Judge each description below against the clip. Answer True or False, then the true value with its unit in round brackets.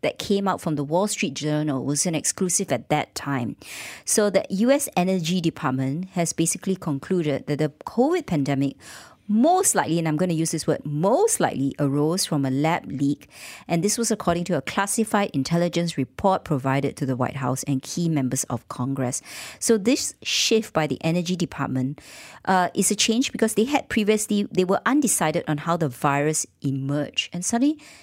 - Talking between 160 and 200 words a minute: True (185 wpm)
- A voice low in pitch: False (170 Hz)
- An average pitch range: False (5.9 semitones)